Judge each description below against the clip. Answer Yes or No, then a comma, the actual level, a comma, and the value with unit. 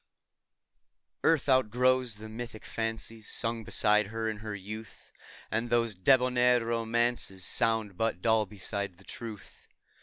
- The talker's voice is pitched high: No, low, 115 Hz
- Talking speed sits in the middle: No, slow, 125 wpm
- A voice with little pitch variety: Yes, narrow, 2.1 semitones